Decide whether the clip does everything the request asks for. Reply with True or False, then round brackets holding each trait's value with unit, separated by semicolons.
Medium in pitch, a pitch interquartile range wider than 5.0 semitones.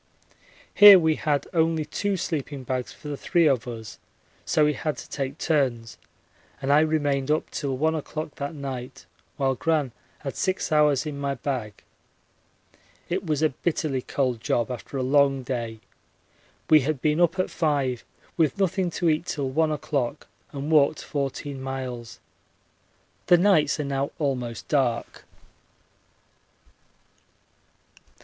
False (145 Hz; 3.1 semitones)